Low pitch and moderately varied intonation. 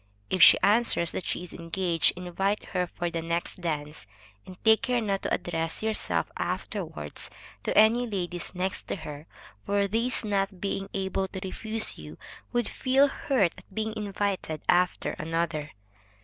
No: high, 190 Hz; average, 4.0 semitones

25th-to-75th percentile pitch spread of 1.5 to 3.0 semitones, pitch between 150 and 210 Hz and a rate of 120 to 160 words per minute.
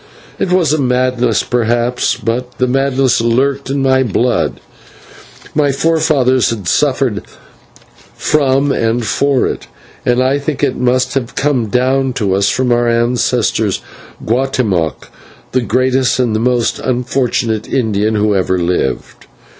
No: narrow, 2.6 semitones; low, 125 Hz; slow, 135 wpm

